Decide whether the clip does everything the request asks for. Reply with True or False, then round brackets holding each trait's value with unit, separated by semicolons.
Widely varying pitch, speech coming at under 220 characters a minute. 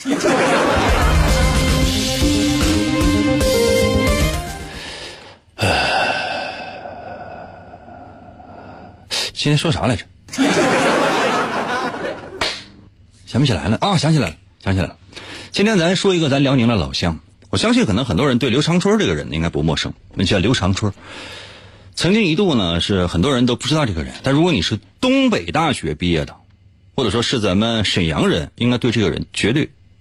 True (6.2 semitones; 210 characters per minute)